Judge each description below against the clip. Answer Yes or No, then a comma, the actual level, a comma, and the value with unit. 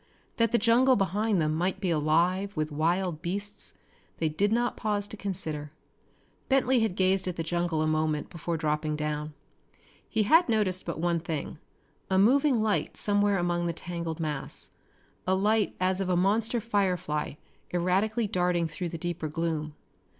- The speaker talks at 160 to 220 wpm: Yes, average, 165 wpm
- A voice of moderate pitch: Yes, medium, 180 Hz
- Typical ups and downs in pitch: Yes, average, 4.3 semitones